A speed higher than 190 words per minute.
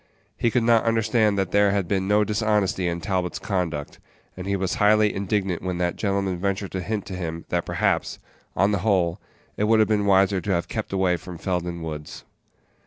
Yes: average, 200 wpm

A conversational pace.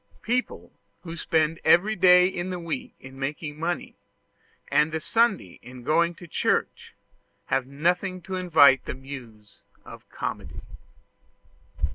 No: slow, 130 wpm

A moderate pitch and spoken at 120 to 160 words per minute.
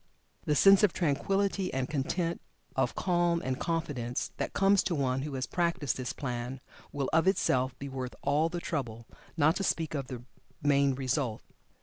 No: medium, 145 Hz; average, 175 wpm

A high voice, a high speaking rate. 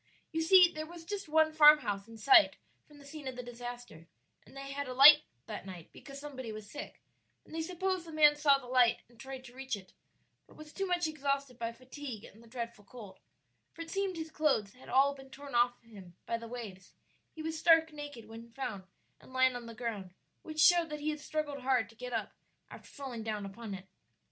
Yes: very high, 265 Hz; fast, 220 wpm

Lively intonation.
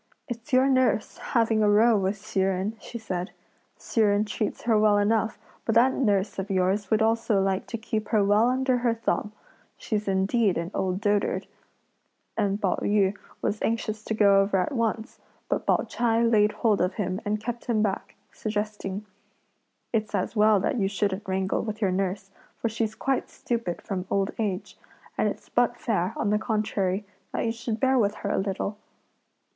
No: narrow, 2.5 semitones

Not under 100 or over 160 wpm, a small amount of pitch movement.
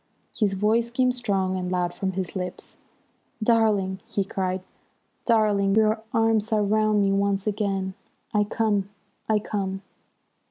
Yes: slow, 135 wpm; narrow, 2.2 semitones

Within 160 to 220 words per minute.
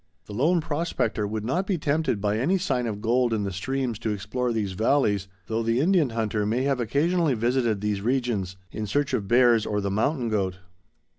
Yes: average, 200 wpm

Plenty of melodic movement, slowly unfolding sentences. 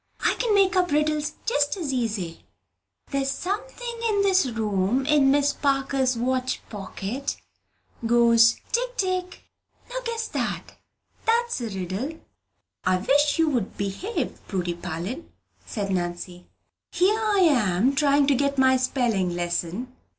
Yes: wide, 8.9 semitones; slow, 130 wpm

